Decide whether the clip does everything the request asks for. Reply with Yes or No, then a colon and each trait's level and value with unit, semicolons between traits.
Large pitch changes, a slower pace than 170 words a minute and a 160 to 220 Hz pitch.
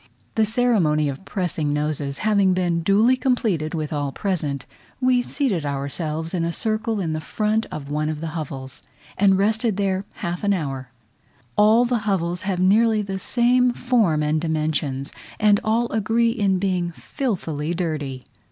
Yes: wide, 5.9 semitones; average, 160 wpm; medium, 185 Hz